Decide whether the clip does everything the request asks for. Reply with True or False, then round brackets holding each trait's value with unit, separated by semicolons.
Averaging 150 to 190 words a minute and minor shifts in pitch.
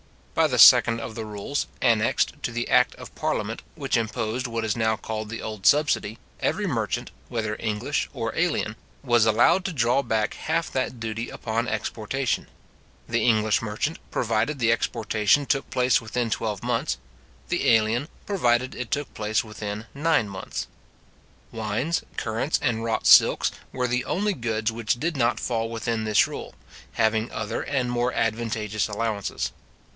True (160 wpm; 2.3 semitones)